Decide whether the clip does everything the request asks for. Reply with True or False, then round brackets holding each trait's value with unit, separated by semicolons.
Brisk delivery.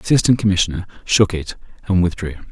False (165 wpm)